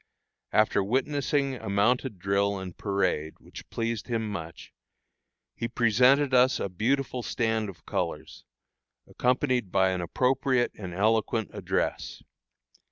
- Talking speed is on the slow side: Yes, slow, 120 wpm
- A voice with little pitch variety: No, average, 4.5 semitones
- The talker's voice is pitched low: Yes, low, 110 Hz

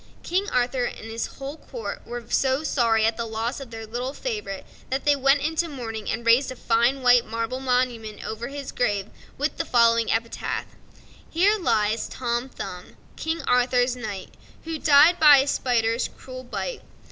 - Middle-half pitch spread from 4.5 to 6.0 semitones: No, average, 3.3 semitones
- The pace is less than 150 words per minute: No, average, 170 wpm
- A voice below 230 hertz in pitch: No, high, 245 Hz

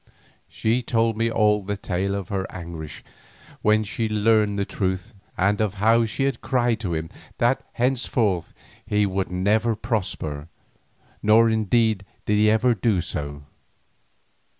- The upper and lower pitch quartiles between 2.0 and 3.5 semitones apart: Yes, average, 3.2 semitones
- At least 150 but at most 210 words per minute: No, average, 140 wpm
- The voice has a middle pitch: No, low, 105 Hz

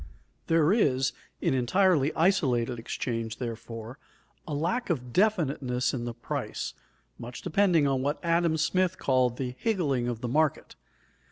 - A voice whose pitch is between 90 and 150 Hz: Yes, low, 135 Hz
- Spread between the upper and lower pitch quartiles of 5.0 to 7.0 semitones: Yes, wide, 5.5 semitones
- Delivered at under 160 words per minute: Yes, average, 140 wpm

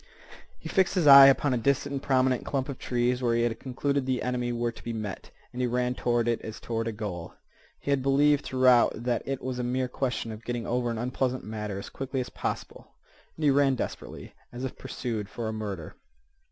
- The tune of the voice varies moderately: No, narrow, 2.3 semitones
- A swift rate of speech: Yes, fast, 220 wpm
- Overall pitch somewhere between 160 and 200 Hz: No, low, 125 Hz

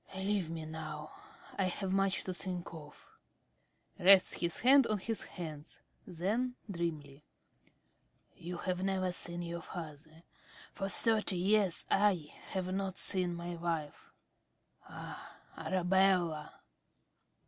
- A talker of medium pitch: Yes, medium, 180 Hz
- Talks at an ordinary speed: No, slow, 115 wpm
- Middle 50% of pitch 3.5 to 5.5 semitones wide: No, average, 2.8 semitones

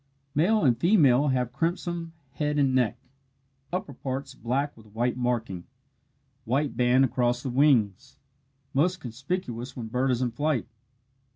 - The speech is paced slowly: Yes, slow, 130 wpm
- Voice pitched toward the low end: Yes, low, 130 Hz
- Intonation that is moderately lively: Yes, average, 3.4 semitones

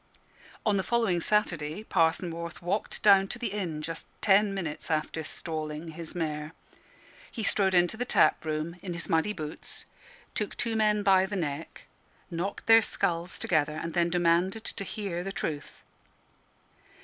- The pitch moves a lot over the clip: No, average, 3.8 semitones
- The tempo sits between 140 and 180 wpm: Yes, average, 160 wpm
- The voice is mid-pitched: Yes, medium, 175 Hz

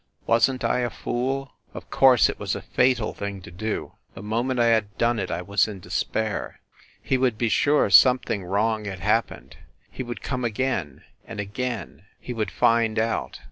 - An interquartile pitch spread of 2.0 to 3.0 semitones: No, average, 3.6 semitones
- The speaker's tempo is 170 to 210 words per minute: Yes, average, 185 wpm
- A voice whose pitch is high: No, low, 115 Hz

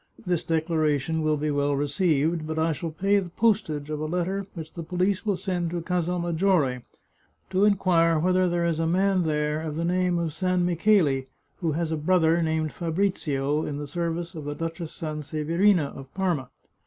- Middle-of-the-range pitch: Yes, medium, 165 Hz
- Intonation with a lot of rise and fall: No, average, 2.8 semitones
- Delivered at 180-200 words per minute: Yes, average, 185 wpm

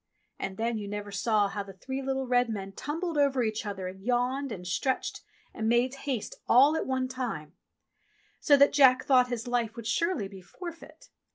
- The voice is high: Yes, high, 245 Hz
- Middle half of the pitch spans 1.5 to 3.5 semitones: No, average, 4.6 semitones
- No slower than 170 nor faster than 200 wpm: Yes, average, 190 wpm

